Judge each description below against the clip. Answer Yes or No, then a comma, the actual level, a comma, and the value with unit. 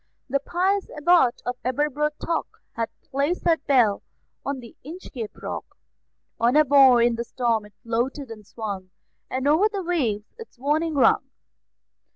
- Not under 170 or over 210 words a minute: No, average, 150 wpm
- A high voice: Yes, very high, 270 Hz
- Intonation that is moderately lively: Yes, average, 4.6 semitones